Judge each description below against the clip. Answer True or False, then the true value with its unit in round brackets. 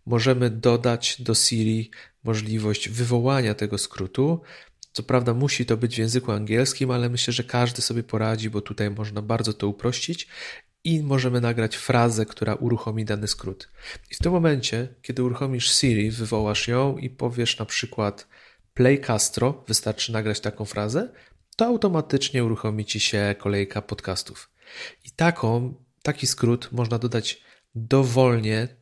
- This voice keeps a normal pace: True (145 wpm)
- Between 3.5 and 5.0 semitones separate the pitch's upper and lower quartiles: False (3.0 semitones)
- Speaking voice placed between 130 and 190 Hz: False (120 Hz)